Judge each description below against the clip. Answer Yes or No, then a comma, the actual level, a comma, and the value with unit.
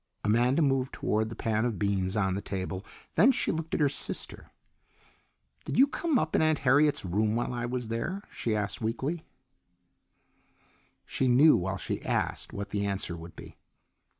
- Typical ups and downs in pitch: No, wide, 6.2 semitones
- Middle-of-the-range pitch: No, low, 115 Hz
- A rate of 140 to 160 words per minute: No, average, 175 wpm